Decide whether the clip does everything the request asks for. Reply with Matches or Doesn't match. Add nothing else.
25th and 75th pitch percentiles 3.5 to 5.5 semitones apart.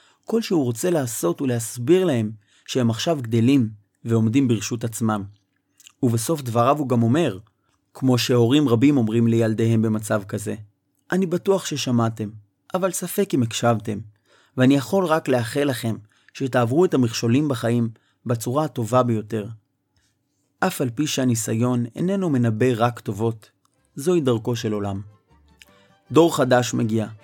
Matches